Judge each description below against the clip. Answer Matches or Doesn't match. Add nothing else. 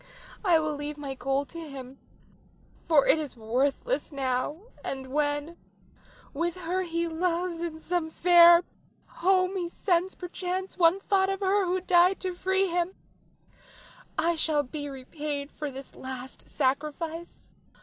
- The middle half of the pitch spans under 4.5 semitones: Matches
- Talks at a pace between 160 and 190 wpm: Doesn't match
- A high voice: Matches